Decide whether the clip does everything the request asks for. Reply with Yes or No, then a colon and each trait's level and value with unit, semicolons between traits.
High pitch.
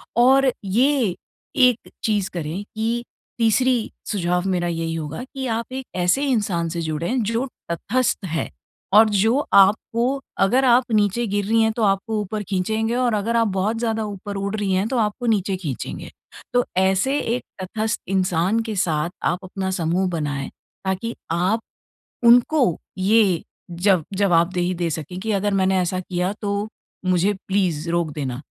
Yes: high, 200 Hz